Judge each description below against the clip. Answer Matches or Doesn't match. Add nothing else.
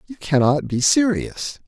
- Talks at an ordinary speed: Matches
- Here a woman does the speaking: Doesn't match